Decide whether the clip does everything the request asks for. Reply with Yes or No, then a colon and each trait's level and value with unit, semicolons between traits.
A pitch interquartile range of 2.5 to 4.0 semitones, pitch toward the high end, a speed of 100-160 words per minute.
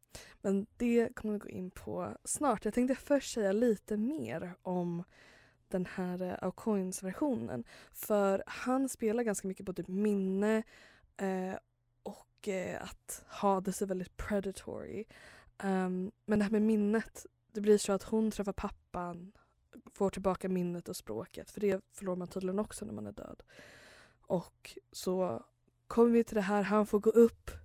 Yes: average, 2.8 semitones; high, 200 Hz; average, 155 wpm